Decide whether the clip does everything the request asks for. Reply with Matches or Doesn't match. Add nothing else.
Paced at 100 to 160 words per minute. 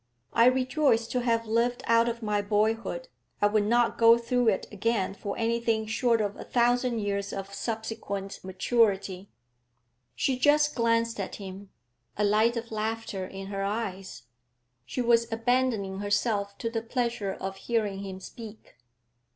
Matches